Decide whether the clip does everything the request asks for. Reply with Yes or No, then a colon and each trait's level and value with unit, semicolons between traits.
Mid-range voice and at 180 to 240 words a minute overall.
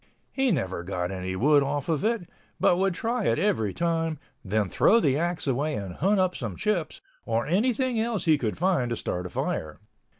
Yes: medium, 155 Hz; average, 200 wpm